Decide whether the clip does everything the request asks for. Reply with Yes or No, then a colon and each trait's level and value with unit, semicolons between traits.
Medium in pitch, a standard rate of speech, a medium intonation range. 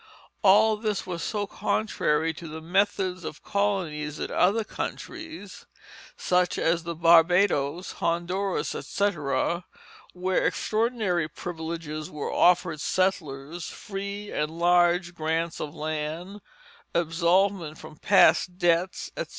No: medium, 175 Hz; slow, 110 wpm; average, 3.5 semitones